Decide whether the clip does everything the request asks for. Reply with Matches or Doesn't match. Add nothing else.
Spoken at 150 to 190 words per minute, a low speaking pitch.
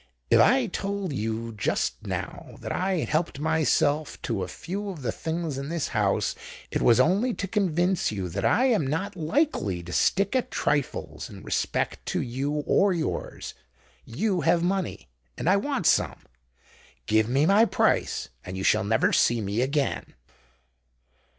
Doesn't match